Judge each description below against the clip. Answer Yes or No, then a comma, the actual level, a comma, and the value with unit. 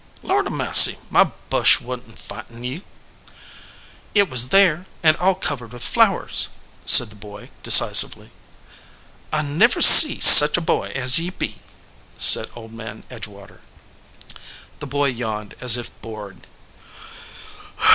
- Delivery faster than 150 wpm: No, slow, 135 wpm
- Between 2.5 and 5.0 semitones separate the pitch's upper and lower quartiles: No, wide, 5.4 semitones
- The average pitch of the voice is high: No, low, 125 Hz